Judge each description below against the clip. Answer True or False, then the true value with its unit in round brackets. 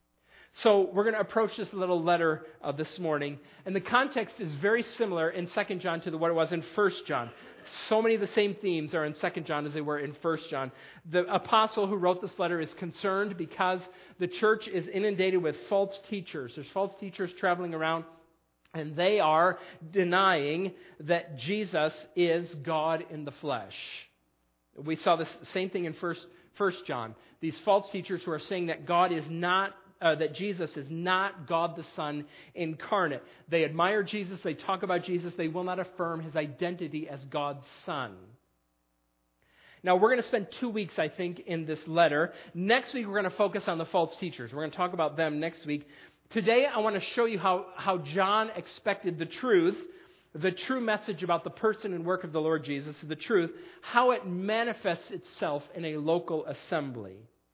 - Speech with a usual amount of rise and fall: True (3.7 semitones)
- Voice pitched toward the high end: False (175 Hz)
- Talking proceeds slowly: False (190 wpm)